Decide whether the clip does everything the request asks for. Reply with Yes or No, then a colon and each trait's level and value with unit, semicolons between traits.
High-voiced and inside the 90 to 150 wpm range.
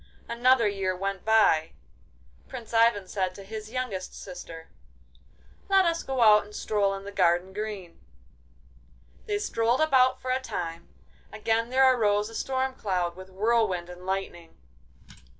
Yes: high, 210 Hz; average, 145 wpm